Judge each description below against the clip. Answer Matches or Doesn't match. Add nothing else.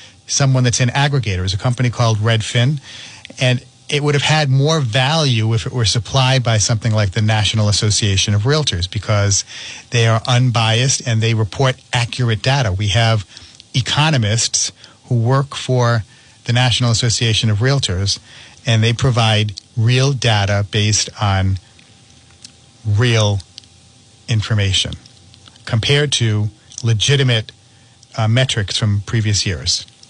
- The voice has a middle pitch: Doesn't match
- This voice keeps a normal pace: Doesn't match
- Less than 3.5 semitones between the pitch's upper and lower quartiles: Matches